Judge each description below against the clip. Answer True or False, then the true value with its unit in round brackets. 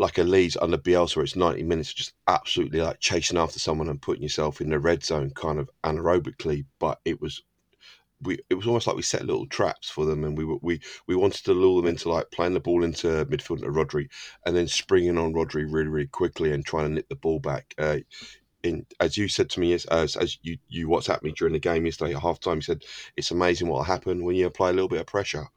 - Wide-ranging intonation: False (2.5 semitones)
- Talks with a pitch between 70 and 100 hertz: True (85 Hz)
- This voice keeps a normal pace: False (245 wpm)